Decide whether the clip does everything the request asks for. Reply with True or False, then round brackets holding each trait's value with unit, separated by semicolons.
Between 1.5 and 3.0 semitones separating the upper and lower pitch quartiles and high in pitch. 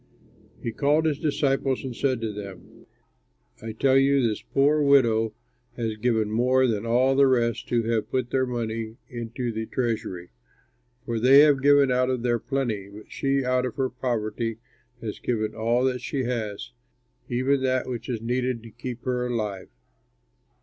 False (2.7 semitones; 125 Hz)